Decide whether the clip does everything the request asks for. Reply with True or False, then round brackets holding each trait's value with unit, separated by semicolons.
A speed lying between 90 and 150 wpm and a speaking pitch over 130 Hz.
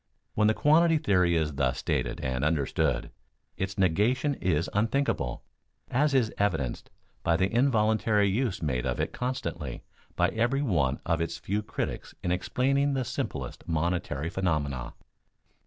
False (140 wpm; 95 Hz)